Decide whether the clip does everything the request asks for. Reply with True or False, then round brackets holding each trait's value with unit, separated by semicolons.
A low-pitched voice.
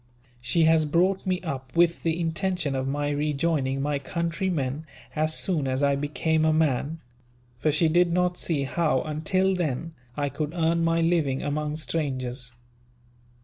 False (155 Hz)